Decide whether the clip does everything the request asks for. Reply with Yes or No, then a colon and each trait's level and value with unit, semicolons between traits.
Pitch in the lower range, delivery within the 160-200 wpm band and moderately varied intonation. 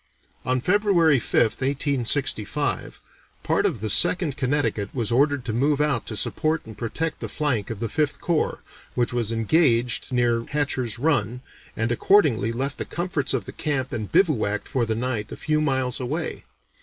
Yes: low, 130 Hz; average, 170 wpm; average, 4.4 semitones